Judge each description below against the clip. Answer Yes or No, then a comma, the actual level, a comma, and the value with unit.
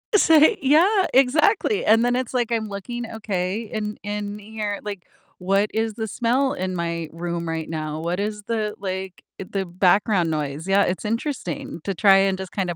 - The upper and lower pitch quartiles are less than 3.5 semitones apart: No, average, 4.1 semitones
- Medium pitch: No, high, 205 Hz